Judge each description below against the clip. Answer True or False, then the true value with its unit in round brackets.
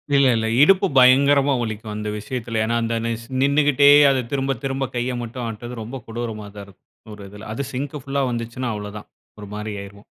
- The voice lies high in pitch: False (120 Hz)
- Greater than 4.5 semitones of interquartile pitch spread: False (3.9 semitones)